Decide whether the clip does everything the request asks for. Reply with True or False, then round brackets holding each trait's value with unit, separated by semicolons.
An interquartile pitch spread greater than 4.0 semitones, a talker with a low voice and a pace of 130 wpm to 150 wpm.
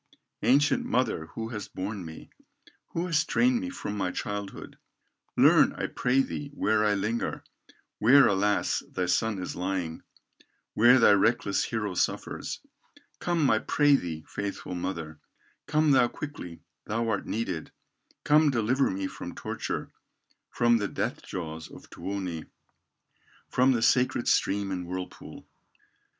True (5.3 semitones; 105 Hz; 135 wpm)